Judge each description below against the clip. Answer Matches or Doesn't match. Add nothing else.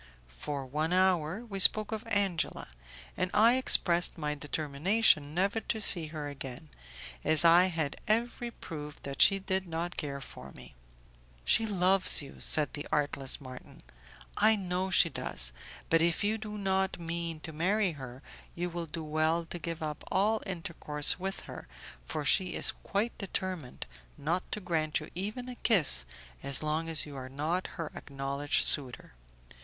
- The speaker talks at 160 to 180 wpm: Matches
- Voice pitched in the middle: Matches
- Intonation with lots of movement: Doesn't match